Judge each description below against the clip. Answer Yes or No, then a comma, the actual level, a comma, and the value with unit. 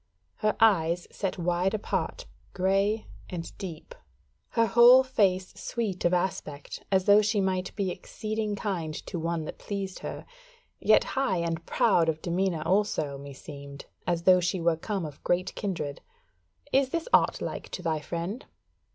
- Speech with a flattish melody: No, average, 3.7 semitones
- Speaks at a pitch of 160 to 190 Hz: Yes, medium, 185 Hz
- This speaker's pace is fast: No, average, 155 wpm